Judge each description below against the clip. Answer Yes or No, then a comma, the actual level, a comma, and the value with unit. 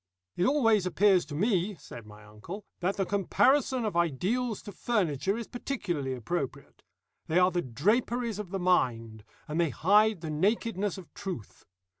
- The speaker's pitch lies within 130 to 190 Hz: Yes, medium, 185 Hz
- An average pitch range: No, wide, 5.9 semitones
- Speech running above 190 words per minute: No, average, 160 wpm